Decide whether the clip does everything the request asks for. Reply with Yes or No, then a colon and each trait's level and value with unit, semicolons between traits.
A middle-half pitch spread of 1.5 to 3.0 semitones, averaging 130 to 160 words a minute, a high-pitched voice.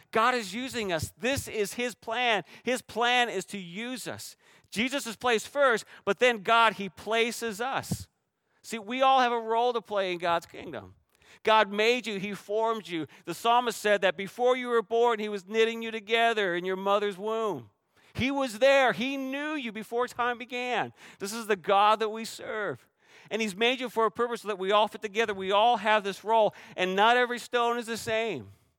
No: average, 2.7 semitones; fast, 205 wpm; high, 225 Hz